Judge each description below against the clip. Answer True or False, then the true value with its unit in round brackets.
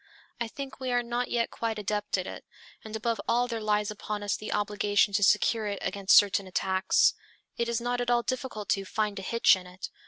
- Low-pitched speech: False (215 Hz)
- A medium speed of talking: False (220 wpm)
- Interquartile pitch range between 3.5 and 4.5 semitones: False (2.7 semitones)